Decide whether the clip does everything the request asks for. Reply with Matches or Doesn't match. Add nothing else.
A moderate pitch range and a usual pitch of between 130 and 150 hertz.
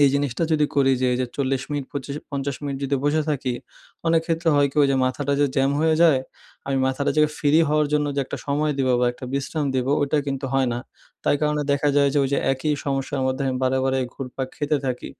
Doesn't match